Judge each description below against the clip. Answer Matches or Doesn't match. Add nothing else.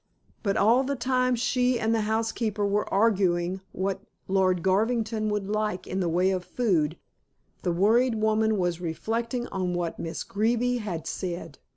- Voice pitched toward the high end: Matches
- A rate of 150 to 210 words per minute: Matches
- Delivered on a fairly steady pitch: Doesn't match